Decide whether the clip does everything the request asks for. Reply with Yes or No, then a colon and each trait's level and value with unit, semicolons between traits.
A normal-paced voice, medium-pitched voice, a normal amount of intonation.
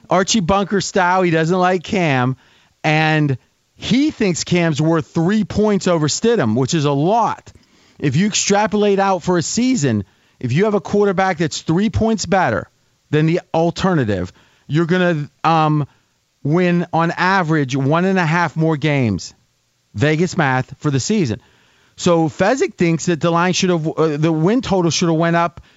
Yes: average, 170 wpm; medium, 170 Hz; average, 3.9 semitones